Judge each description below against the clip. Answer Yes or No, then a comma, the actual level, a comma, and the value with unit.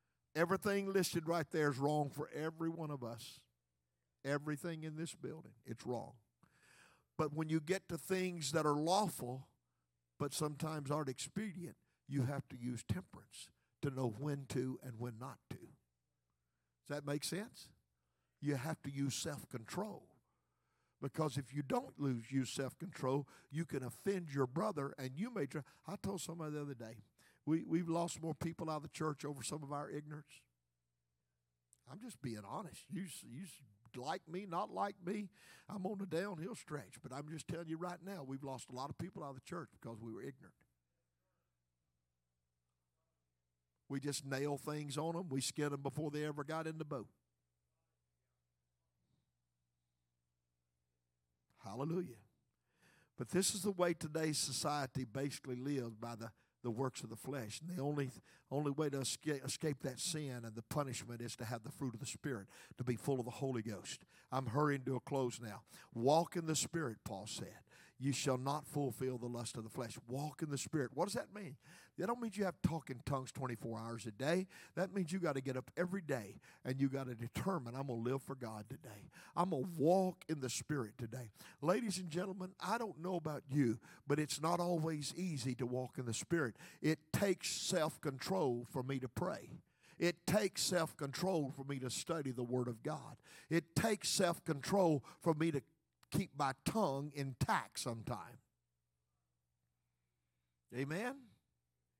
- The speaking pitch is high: No, medium, 140 Hz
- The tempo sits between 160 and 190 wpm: Yes, average, 180 wpm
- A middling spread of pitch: No, wide, 5.7 semitones